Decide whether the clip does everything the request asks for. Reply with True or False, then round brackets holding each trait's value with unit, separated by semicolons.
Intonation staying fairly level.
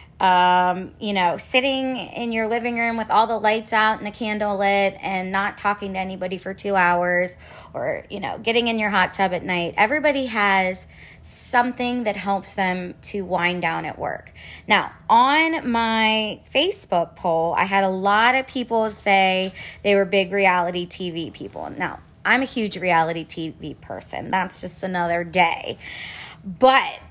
False (3.6 semitones)